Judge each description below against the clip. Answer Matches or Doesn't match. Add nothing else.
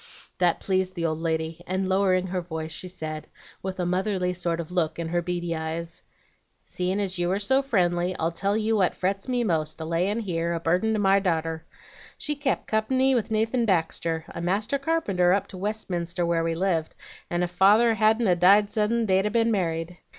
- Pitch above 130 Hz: Matches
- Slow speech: Doesn't match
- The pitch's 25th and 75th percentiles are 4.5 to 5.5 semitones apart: Doesn't match